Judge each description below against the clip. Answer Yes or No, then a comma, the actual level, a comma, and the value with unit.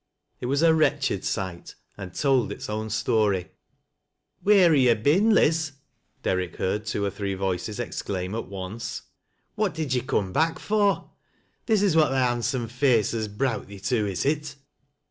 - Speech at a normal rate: Yes, average, 180 wpm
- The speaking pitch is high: No, low, 120 Hz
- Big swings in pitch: Yes, wide, 6.9 semitones